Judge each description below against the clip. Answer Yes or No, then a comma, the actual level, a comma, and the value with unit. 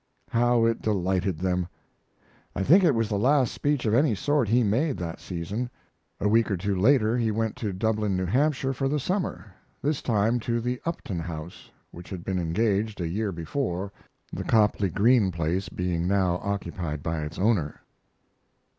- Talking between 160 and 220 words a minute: Yes, average, 175 wpm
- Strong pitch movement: No, average, 5.0 semitones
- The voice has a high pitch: No, low, 105 Hz